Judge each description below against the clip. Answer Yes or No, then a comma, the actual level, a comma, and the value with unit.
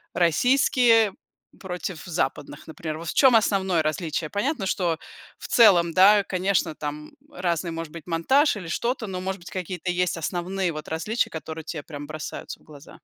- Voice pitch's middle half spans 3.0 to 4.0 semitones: Yes, average, 3.6 semitones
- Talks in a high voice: No, medium, 180 Hz